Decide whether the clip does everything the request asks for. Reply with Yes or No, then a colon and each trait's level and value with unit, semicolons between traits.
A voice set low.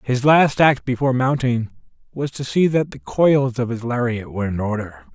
Yes: low, 125 Hz